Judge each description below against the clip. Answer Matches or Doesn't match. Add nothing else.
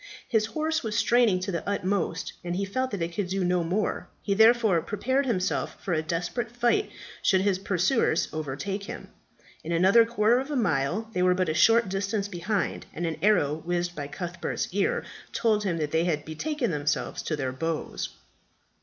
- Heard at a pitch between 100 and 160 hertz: Doesn't match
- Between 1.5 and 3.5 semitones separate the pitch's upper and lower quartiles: Doesn't match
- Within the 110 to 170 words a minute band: Doesn't match